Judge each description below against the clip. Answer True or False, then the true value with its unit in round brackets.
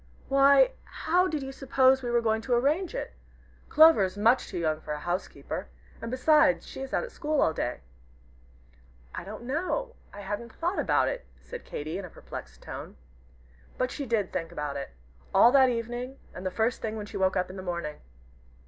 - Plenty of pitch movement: True (6.9 semitones)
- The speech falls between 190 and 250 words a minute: True (195 wpm)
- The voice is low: False (235 Hz)